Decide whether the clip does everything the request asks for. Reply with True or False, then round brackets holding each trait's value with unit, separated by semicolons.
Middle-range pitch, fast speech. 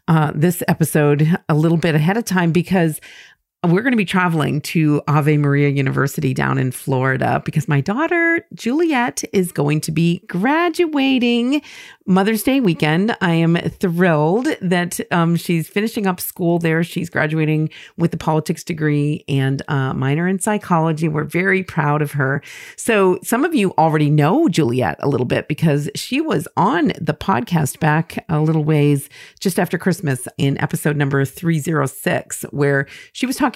False (165 Hz; 165 wpm)